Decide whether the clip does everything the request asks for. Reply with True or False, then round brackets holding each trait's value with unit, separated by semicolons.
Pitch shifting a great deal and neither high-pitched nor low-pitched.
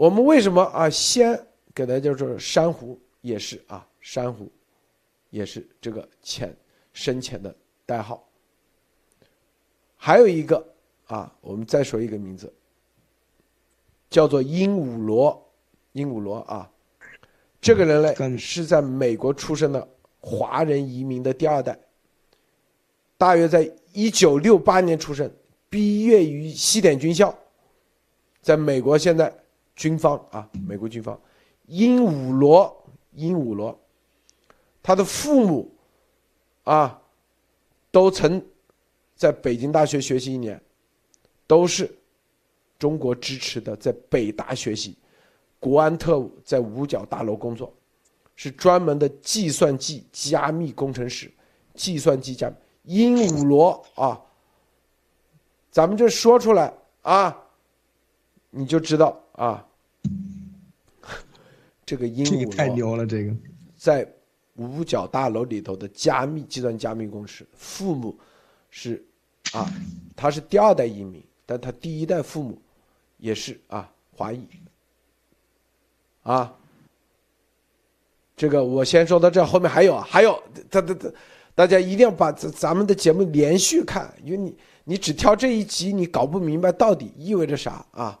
True (6.3 semitones; 150 Hz)